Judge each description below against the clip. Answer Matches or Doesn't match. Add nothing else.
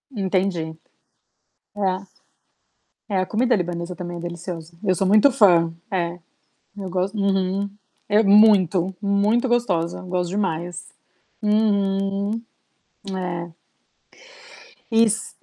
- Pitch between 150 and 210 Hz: Matches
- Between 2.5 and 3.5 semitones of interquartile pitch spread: Matches